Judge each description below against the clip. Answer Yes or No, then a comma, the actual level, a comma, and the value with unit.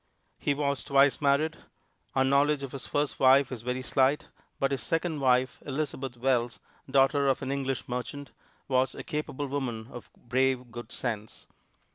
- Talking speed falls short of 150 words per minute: No, average, 160 wpm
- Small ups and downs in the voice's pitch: Yes, narrow, 1.9 semitones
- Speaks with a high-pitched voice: No, low, 135 Hz